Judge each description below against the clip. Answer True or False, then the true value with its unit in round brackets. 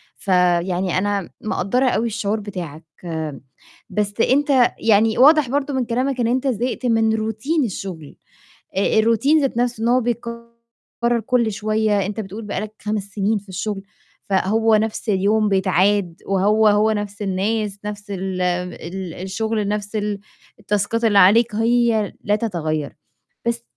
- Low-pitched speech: False (210 Hz)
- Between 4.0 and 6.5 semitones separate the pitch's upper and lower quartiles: False (2.9 semitones)